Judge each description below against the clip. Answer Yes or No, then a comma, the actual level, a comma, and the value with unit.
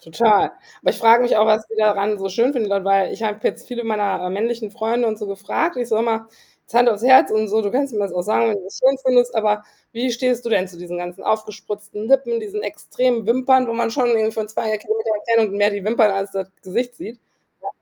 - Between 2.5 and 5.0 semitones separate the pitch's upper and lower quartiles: Yes, average, 2.8 semitones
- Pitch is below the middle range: No, high, 220 Hz